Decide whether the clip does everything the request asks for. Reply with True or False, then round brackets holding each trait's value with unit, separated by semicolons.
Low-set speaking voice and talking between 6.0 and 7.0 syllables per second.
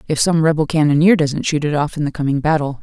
False (150 Hz; 6.4 syllables/s)